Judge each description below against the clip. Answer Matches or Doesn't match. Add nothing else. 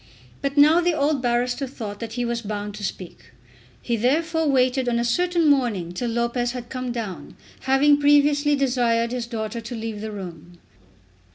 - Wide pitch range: Doesn't match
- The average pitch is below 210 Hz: Doesn't match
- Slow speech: Doesn't match